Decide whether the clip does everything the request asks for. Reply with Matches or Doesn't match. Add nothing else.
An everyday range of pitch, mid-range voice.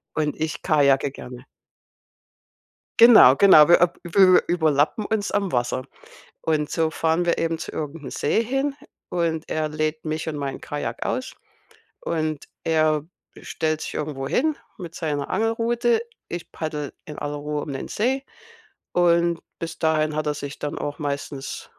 Matches